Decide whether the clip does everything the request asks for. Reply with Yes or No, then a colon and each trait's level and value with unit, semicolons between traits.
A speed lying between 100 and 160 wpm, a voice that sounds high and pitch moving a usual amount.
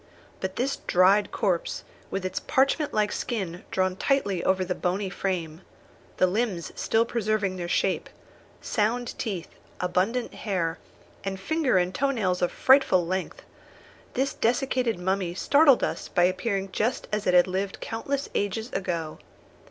Yes: average, 145 wpm; high, 195 Hz; average, 4.3 semitones